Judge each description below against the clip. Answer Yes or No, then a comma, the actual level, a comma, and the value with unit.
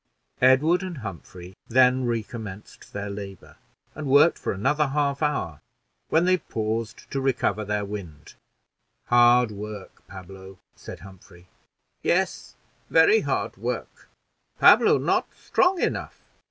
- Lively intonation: Yes, wide, 6.0 semitones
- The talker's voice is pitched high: No, low, 115 Hz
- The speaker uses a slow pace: Yes, slow, 120 wpm